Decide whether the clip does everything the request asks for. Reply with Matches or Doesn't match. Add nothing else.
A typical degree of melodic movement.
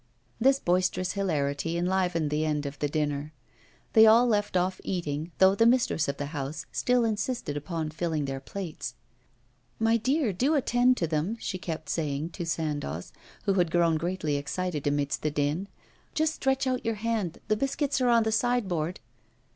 Doesn't match